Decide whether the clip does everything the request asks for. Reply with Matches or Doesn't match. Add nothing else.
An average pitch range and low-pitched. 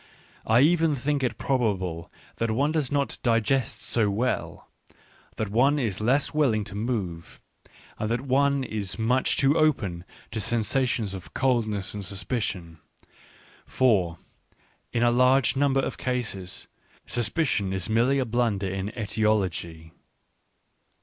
Matches